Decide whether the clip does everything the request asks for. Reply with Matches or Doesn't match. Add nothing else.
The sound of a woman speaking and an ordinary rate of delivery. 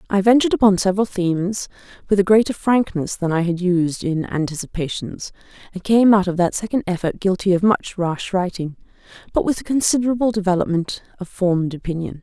Matches